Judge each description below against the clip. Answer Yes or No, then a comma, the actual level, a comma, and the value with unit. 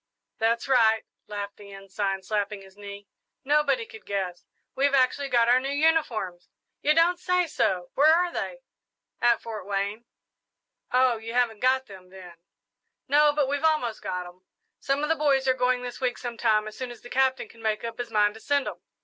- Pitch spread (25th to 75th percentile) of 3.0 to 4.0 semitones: No, average, 5.3 semitones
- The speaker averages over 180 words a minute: Yes, average, 190 wpm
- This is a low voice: No, high, 240 Hz